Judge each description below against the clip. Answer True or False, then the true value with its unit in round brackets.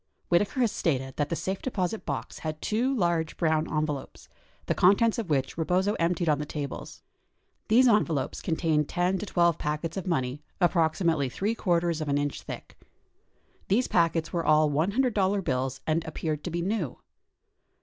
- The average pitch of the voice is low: False (170 Hz)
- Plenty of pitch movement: False (4.0 semitones)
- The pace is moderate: True (165 wpm)